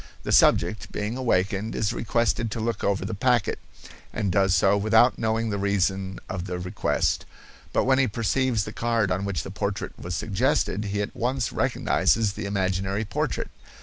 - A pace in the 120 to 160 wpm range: No, average, 175 wpm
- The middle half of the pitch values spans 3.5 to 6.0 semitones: No, average, 2.8 semitones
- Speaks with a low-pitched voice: Yes, low, 105 Hz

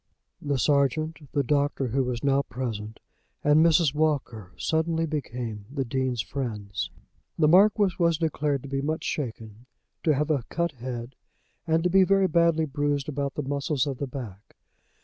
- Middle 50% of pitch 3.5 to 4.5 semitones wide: Yes, average, 3.8 semitones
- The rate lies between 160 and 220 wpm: Yes, average, 165 wpm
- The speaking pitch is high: No, medium, 140 Hz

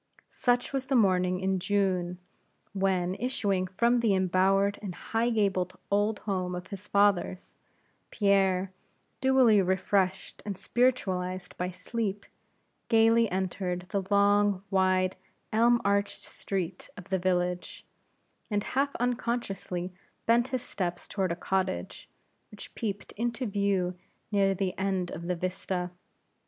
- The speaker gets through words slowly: Yes, slow, 125 wpm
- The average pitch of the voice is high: Yes, high, 195 Hz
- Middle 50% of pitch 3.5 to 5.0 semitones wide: No, average, 2.7 semitones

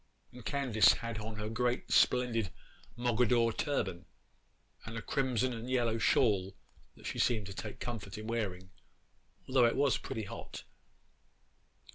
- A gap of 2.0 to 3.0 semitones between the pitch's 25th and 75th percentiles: Yes, average, 2.7 semitones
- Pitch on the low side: Yes, low, 115 Hz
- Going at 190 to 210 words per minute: No, average, 140 wpm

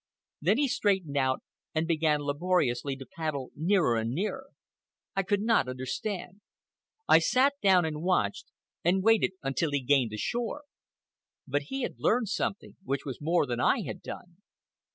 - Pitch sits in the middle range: Yes, medium, 165 Hz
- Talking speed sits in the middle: Yes, average, 160 wpm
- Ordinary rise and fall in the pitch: No, wide, 6.3 semitones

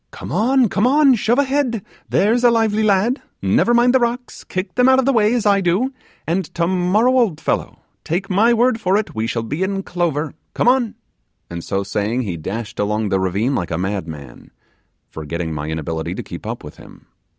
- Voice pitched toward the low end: No, high, 190 Hz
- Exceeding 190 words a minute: Yes, average, 200 wpm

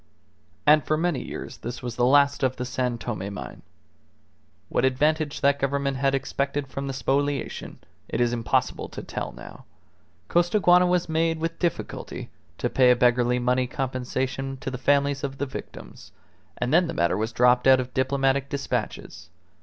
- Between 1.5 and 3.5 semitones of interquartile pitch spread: Yes, narrow, 2.4 semitones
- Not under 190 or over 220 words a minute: No, average, 165 wpm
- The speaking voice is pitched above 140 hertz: No, low, 135 Hz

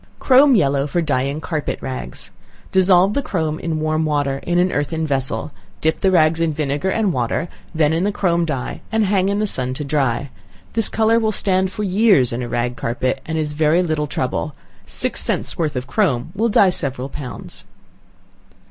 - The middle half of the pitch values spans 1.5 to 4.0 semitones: No, average, 5.3 semitones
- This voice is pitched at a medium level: Yes, medium, 155 Hz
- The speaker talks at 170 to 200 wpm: Yes, average, 190 wpm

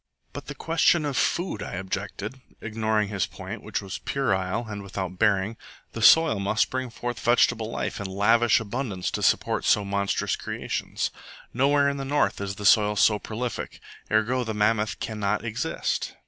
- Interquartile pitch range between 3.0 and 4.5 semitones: Yes, average, 3.4 semitones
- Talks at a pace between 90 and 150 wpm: No, average, 165 wpm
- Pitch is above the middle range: No, low, 110 Hz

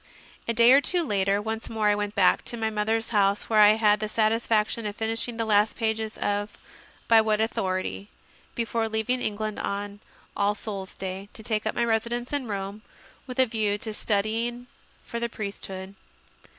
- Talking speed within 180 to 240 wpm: Yes, average, 185 wpm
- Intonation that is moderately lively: No, narrow, 1.8 semitones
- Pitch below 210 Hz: No, high, 215 Hz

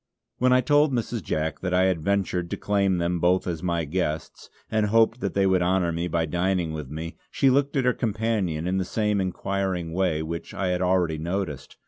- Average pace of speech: No, fast, 210 wpm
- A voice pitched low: Yes, very low, 90 Hz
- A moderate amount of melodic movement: Yes, average, 3.4 semitones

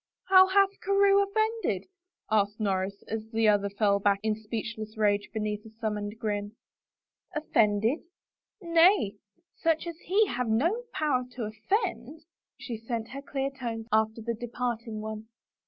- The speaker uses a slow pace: No, average, 155 wpm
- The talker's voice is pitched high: Yes, high, 225 Hz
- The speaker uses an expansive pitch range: Yes, wide, 7.0 semitones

